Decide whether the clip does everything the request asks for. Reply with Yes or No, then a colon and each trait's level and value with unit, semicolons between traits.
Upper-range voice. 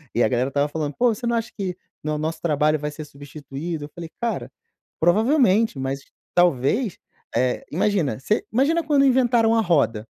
No: medium, 165 Hz